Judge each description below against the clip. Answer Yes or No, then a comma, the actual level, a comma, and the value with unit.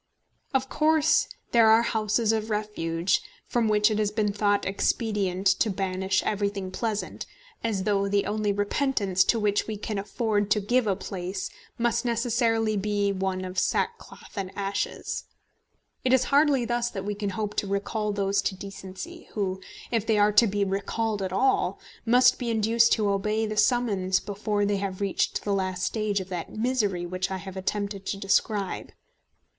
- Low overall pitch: No, high, 205 Hz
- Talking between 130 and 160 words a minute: No, average, 170 wpm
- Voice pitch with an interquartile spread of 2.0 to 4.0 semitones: Yes, narrow, 2.4 semitones